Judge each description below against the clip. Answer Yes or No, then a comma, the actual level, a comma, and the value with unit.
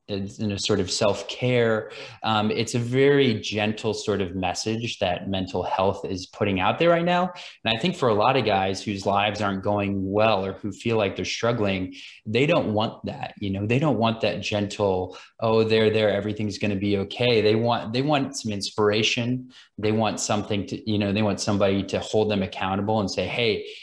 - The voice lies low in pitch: Yes, low, 105 Hz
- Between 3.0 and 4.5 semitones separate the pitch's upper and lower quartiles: No, narrow, 2.6 semitones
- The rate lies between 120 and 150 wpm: No, fast, 205 wpm